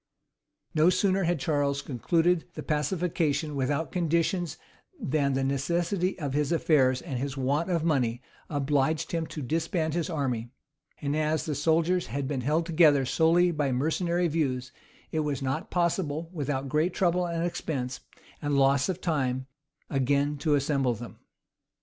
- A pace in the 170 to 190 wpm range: No, average, 150 wpm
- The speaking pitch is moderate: Yes, medium, 150 Hz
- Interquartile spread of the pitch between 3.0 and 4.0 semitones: Yes, average, 3.6 semitones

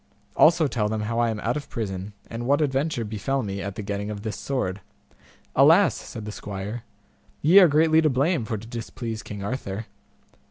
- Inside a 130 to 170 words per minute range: No, average, 195 wpm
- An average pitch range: Yes, average, 4.6 semitones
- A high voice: No, low, 115 Hz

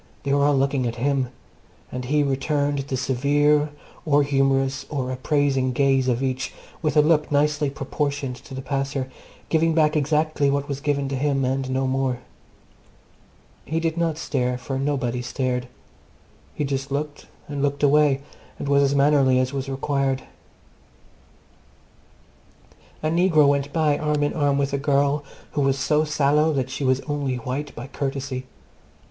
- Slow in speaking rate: No, average, 160 wpm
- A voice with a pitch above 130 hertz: Yes, medium, 140 Hz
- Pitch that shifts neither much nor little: No, narrow, 1.7 semitones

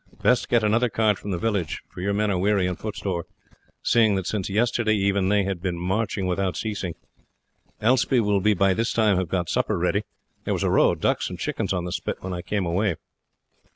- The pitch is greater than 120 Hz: No, low, 100 Hz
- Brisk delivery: Yes, fast, 215 wpm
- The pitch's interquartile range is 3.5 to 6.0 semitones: No, average, 2.8 semitones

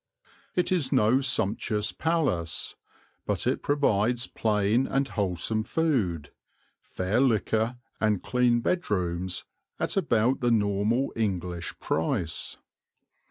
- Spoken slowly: Yes, slow, 105 wpm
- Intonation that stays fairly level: No, average, 4.9 semitones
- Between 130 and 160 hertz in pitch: No, low, 110 Hz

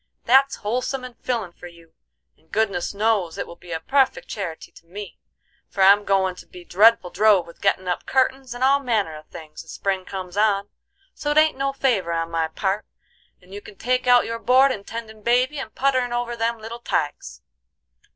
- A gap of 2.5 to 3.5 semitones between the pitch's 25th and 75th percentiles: No, wide, 5.4 semitones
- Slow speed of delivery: No, average, 200 wpm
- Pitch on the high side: Yes, high, 215 Hz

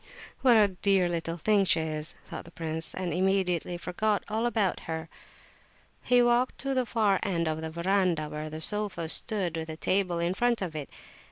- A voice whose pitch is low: No, medium, 180 Hz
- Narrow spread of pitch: No, average, 4.4 semitones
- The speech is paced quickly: No, average, 190 wpm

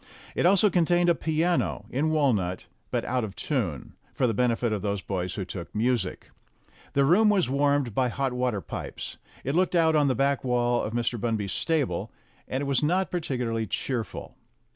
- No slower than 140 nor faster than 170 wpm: No, average, 185 wpm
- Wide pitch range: Yes, wide, 5.7 semitones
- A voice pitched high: No, low, 130 Hz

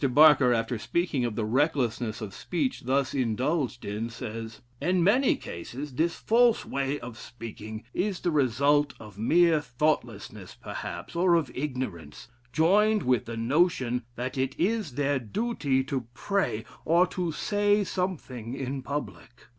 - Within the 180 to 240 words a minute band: No, average, 145 wpm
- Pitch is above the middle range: No, low, 135 Hz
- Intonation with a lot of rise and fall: Yes, wide, 6.2 semitones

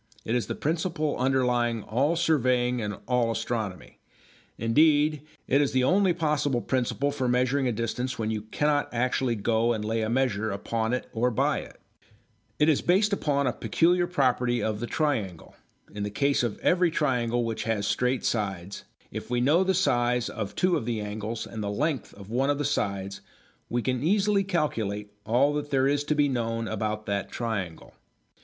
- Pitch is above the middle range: No, low, 125 Hz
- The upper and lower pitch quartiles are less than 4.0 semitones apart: No, average, 4.7 semitones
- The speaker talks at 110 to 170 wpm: No, average, 185 wpm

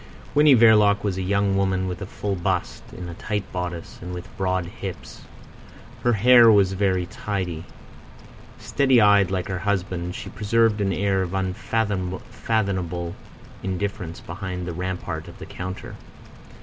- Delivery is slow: No, average, 150 wpm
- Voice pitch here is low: Yes, very low, 95 Hz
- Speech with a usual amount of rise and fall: No, narrow, 2.3 semitones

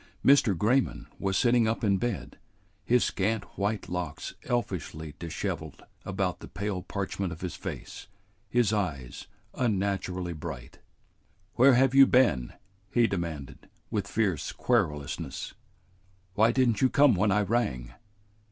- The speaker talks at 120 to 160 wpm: Yes, slow, 135 wpm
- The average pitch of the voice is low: Yes, low, 100 Hz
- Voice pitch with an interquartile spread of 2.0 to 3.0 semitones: No, average, 5.3 semitones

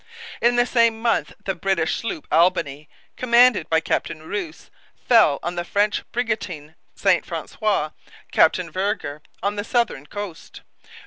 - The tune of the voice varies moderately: No, wide, 6.0 semitones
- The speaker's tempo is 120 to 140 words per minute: Yes, slow, 135 wpm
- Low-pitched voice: No, high, 195 Hz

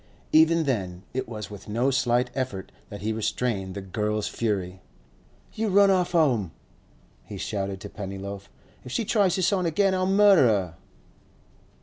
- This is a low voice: Yes, low, 115 Hz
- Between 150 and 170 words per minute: Yes, average, 155 wpm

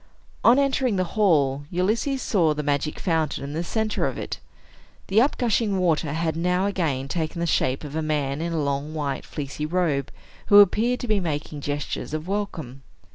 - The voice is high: No, medium, 165 Hz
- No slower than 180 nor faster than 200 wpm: Yes, average, 185 wpm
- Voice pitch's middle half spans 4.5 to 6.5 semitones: Yes, wide, 5.5 semitones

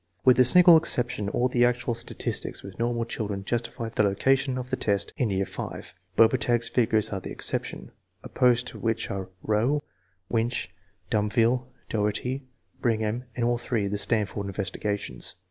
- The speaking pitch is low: Yes, low, 115 Hz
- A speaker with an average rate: Yes, average, 165 wpm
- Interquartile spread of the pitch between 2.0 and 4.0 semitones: Yes, average, 3.1 semitones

